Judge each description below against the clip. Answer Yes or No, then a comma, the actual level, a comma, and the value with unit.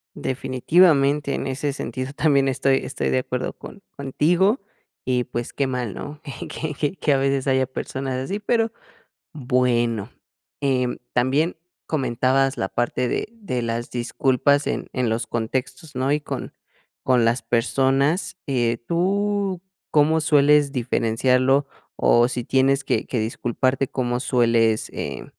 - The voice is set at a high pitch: No, low, 130 Hz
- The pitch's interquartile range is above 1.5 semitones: Yes, average, 2.9 semitones